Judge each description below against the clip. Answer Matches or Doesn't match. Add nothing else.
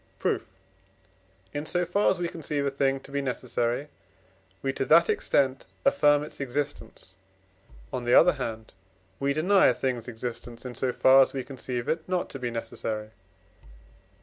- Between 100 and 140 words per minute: Doesn't match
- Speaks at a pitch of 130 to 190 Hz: Matches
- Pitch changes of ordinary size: Matches